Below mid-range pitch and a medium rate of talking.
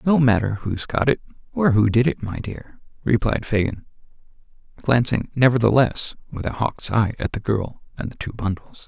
Yes: low, 115 Hz; average, 175 wpm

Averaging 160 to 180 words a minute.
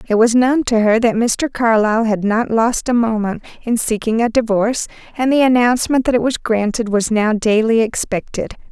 No: average, 195 wpm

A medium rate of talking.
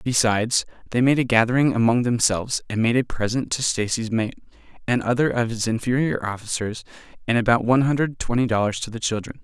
Yes: average, 185 wpm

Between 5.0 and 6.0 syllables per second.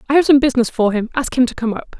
No: 7.4 syllables/s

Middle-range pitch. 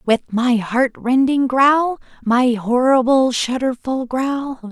No: very high, 255 Hz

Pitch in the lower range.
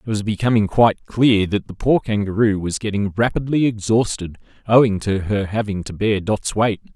Yes: low, 105 Hz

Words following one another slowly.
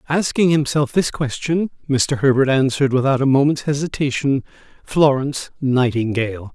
Yes: slow, 120 wpm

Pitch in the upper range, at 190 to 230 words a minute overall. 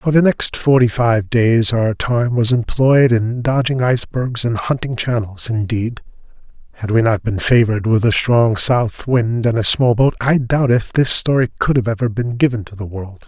No: low, 120 Hz; average, 200 wpm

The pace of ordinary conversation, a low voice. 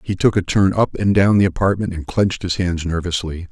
No: fast, 240 wpm; very low, 90 Hz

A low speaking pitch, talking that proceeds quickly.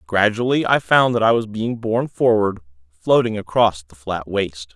No: low, 105 Hz; average, 175 wpm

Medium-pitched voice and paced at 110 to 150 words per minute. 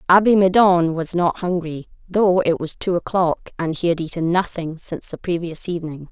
No: medium, 175 Hz; average, 185 wpm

